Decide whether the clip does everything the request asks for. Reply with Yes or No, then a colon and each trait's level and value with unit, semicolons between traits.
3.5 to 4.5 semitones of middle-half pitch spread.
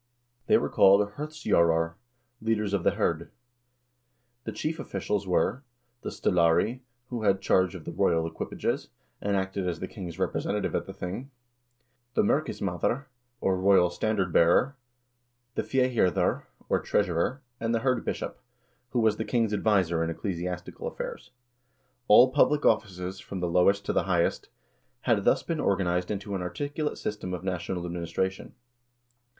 Yes: average, 4.0 semitones